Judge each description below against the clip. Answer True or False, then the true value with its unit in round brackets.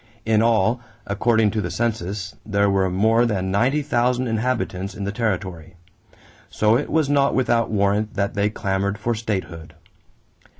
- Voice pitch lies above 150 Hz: False (105 Hz)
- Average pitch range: True (3.0 semitones)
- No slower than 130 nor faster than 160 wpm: True (155 wpm)